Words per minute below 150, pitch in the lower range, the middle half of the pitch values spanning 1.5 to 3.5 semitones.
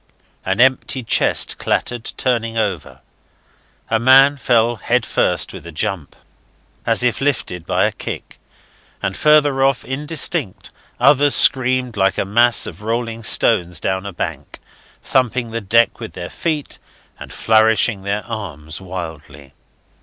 No: average, 140 wpm; low, 115 Hz; average, 5.1 semitones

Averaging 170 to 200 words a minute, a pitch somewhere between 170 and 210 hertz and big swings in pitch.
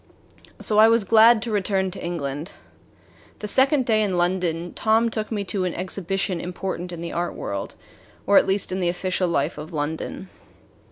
No: average, 180 wpm; high, 190 Hz; average, 3.7 semitones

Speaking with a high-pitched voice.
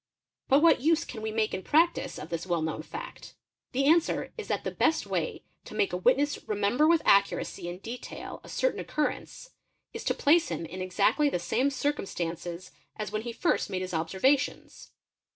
Yes: high, 230 Hz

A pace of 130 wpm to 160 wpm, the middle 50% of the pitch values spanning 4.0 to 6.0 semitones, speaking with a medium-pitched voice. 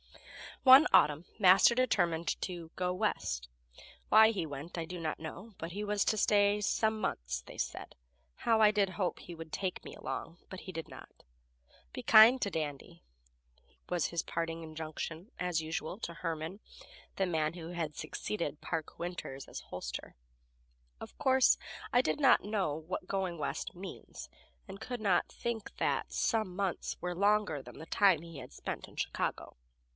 No: average, 170 wpm; average, 4.3 semitones; medium, 180 Hz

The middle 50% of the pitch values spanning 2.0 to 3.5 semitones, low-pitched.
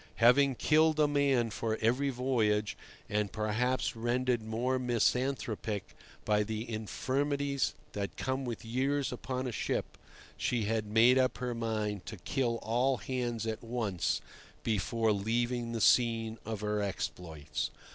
Yes: average, 3.0 semitones; low, 115 Hz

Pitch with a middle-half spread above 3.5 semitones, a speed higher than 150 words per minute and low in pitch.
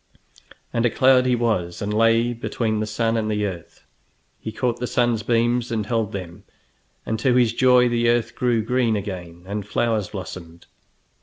No: narrow, 2.5 semitones; average, 175 wpm; low, 115 Hz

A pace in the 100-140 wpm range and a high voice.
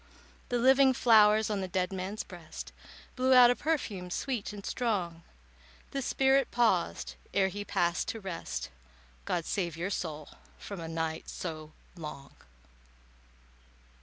Yes: slow, 135 wpm; high, 195 Hz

